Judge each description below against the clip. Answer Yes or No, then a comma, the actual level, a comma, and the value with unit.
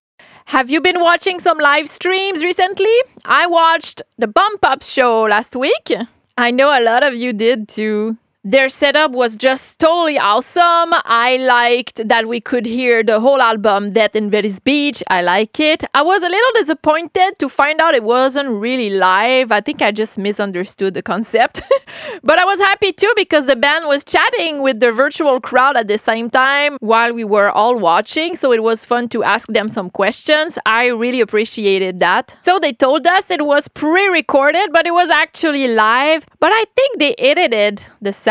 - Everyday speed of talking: Yes, average, 190 wpm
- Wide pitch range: Yes, wide, 6.3 semitones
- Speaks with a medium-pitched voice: No, very high, 265 Hz